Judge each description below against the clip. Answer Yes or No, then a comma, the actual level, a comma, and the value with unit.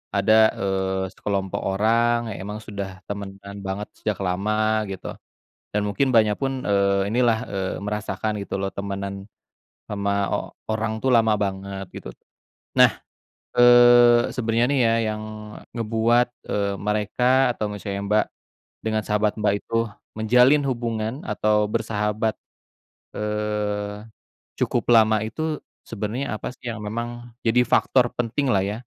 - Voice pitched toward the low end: Yes, low, 105 Hz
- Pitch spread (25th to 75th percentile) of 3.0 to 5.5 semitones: No, narrow, 2.5 semitones